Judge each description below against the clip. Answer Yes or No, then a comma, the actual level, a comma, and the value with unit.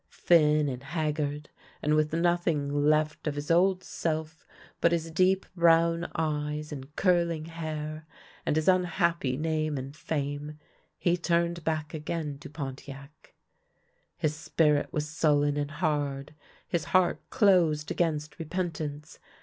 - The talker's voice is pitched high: No, medium, 155 Hz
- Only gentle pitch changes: Yes, narrow, 2.3 semitones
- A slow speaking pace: Yes, slow, 130 wpm